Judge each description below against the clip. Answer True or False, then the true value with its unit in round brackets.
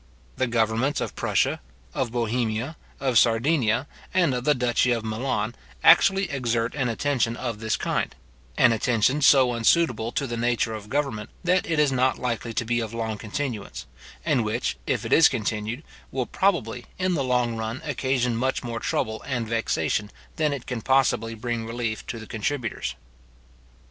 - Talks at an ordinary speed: True (170 wpm)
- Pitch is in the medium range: False (120 Hz)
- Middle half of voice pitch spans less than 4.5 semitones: True (3.0 semitones)